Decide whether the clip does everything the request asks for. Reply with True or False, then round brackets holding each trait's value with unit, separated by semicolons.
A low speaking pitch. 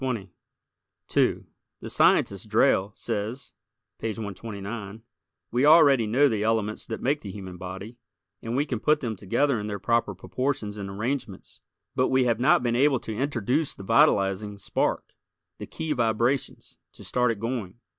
True (115 Hz)